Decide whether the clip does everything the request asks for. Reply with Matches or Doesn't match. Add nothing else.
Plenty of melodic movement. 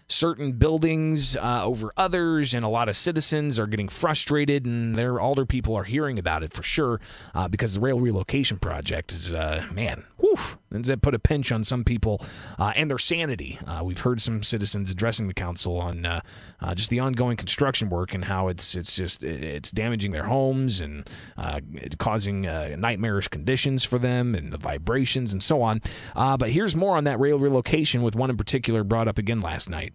Matches